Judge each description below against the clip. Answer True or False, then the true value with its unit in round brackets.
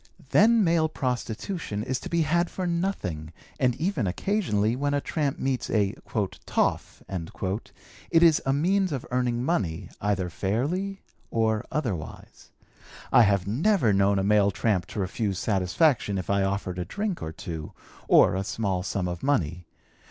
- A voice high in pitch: False (110 Hz)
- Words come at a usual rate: True (155 wpm)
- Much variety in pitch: True (8.4 semitones)